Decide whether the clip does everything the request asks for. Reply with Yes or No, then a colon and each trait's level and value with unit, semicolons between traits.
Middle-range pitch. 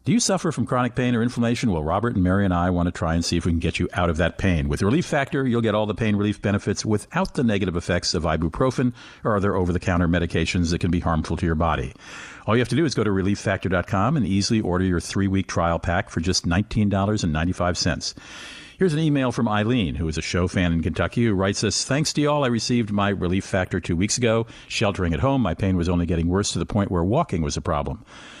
No: very low, 95 Hz